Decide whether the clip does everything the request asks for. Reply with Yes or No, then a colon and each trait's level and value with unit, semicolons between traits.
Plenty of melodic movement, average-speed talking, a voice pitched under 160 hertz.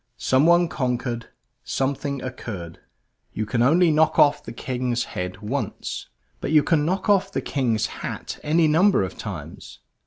No: average, 5.0 semitones; average, 150 wpm; low, 135 Hz